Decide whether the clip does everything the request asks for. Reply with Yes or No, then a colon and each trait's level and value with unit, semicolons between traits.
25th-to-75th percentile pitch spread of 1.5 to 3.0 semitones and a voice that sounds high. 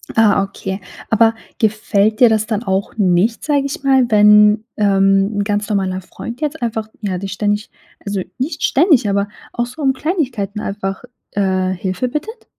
No: average, 3.5 semitones; high, 210 Hz